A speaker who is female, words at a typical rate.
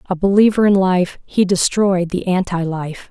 Yes: female; average, 175 wpm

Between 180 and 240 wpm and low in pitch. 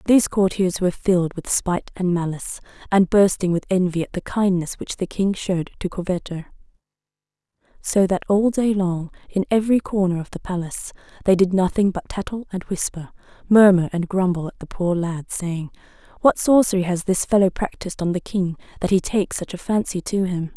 No: average, 185 wpm; medium, 185 Hz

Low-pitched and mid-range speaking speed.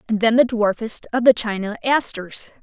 No: high, 225 Hz; average, 185 wpm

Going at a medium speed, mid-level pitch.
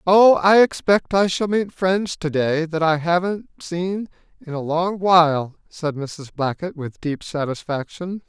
Yes: average, 160 wpm; medium, 170 Hz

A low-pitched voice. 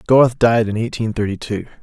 Yes: low, 110 Hz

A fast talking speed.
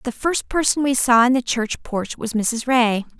Yes: fast, 225 wpm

